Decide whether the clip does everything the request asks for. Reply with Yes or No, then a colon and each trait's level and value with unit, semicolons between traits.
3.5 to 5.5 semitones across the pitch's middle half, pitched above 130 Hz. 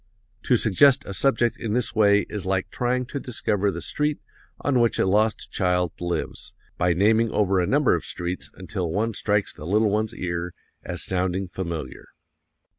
No: average, 4.0 semitones; low, 100 Hz